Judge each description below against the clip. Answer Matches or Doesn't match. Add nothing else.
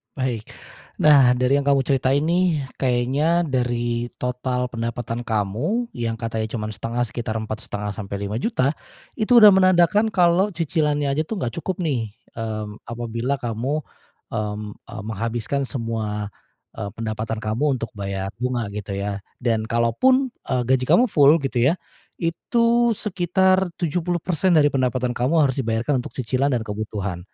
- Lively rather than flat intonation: Matches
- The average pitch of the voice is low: Matches